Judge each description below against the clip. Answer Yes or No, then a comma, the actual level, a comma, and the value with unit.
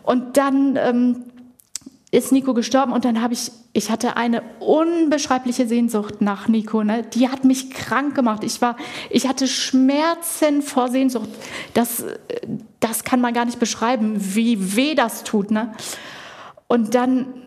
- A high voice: Yes, high, 245 Hz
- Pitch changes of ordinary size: No, narrow, 2.3 semitones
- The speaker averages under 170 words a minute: Yes, average, 150 wpm